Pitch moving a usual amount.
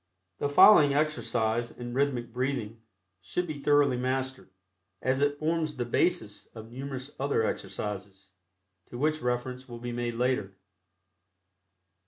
Yes: average, 3.3 semitones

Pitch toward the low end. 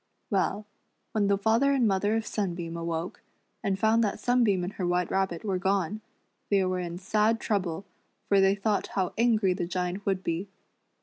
No: high, 195 Hz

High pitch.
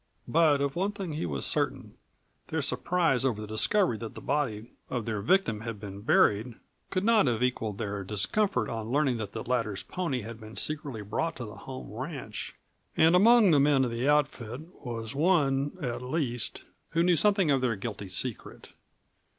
No: low, 125 Hz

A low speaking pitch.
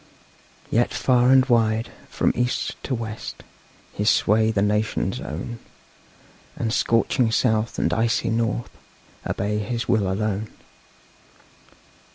Yes: low, 110 Hz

